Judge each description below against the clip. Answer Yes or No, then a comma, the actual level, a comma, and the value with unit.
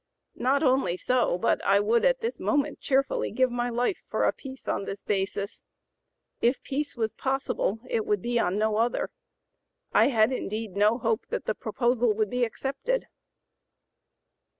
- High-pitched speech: Yes, high, 240 Hz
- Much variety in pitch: No, average, 3.8 semitones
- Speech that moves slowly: No, average, 165 wpm